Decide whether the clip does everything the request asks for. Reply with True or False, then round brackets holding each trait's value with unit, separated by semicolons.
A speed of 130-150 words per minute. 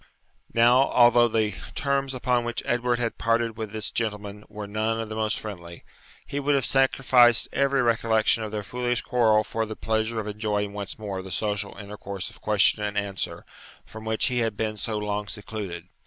False (185 wpm)